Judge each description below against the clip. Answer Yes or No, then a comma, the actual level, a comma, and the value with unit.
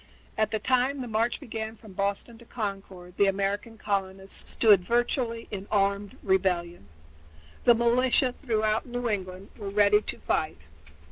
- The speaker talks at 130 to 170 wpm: Yes, average, 145 wpm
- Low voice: No, high, 210 Hz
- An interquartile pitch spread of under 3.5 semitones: Yes, average, 3.1 semitones